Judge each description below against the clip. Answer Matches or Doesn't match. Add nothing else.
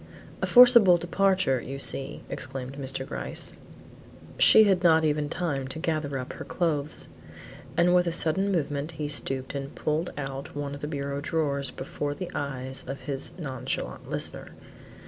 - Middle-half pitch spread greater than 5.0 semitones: Doesn't match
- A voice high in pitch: Doesn't match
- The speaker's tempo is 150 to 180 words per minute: Matches